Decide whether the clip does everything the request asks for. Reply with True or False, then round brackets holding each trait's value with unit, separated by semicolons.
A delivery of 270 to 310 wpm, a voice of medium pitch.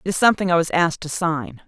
True (285 wpm; 165 Hz)